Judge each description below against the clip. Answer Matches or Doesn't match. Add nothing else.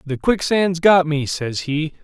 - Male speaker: Matches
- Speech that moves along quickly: Doesn't match